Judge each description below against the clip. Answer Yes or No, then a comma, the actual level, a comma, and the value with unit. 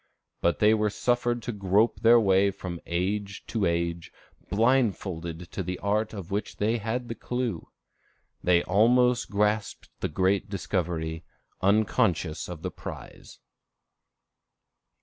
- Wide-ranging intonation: No, average, 4.0 semitones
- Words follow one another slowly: Yes, slow, 130 wpm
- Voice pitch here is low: Yes, low, 100 Hz